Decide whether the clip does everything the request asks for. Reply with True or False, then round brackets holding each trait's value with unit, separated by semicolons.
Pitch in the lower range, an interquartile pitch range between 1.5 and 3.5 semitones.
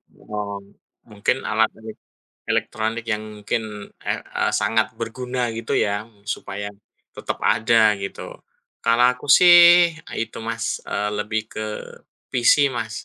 True (110 Hz; 2.4 semitones)